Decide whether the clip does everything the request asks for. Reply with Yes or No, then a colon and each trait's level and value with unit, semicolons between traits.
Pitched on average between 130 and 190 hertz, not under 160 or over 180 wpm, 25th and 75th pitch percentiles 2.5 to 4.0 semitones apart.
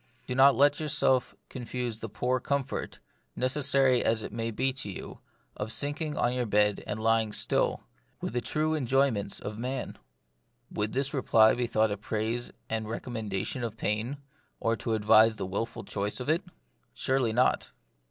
No: low, 120 Hz; average, 170 wpm; average, 3.4 semitones